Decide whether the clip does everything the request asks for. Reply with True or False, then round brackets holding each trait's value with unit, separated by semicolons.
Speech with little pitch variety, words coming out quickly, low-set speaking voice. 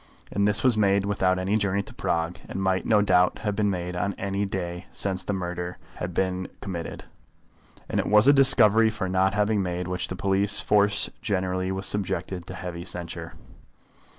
False (2.0 semitones; 185 wpm; 95 Hz)